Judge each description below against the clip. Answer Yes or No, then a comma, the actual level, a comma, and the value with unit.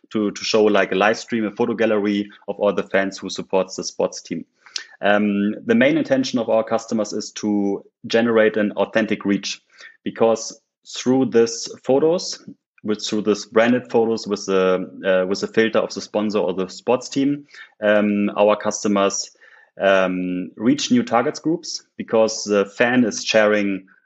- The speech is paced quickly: No, average, 165 wpm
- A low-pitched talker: Yes, low, 105 Hz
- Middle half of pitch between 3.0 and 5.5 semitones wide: No, narrow, 2.5 semitones